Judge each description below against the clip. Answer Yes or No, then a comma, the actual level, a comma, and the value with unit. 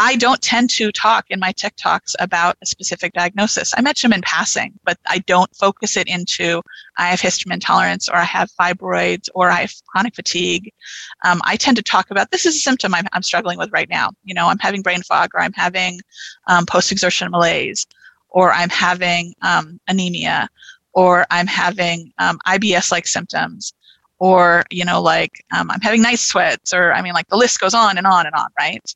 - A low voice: No, medium, 185 Hz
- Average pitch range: Yes, average, 3.1 semitones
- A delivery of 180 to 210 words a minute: Yes, fast, 205 wpm